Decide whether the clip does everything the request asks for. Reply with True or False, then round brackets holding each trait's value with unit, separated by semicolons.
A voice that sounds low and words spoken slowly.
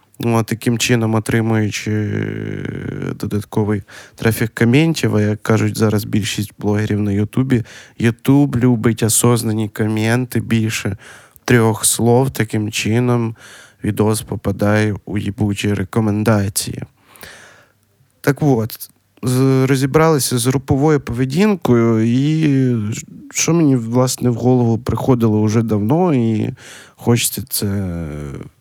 True (115 Hz; 100 wpm)